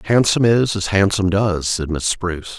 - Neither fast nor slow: Yes, average, 185 wpm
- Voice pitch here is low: Yes, very low, 95 Hz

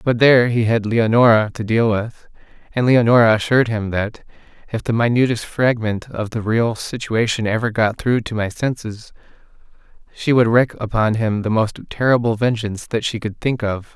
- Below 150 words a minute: No, average, 175 wpm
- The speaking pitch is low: Yes, low, 115 Hz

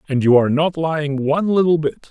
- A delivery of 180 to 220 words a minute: No, fast, 230 wpm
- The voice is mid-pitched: Yes, medium, 150 Hz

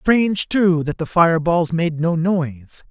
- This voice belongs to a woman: No, male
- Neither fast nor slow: Yes, average, 165 wpm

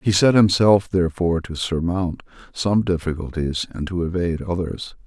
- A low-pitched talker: Yes, very low, 90 Hz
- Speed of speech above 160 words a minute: No, average, 140 wpm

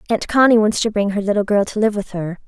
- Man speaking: No, female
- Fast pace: Yes, fast, 290 wpm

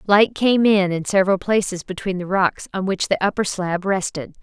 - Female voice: Yes, female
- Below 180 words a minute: No, fast, 205 wpm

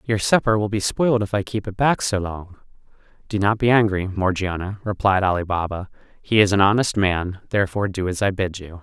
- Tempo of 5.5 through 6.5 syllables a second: Yes, 5.7 syllables/s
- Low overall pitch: Yes, low, 100 Hz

